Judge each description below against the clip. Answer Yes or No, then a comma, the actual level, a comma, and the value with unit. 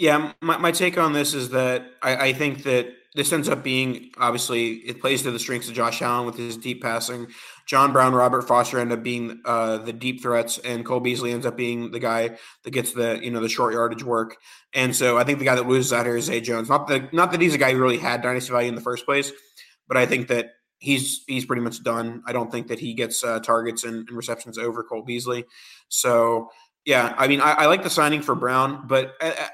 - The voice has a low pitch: Yes, low, 125 Hz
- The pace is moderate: No, fast, 250 wpm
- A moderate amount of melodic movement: No, narrow, 2.1 semitones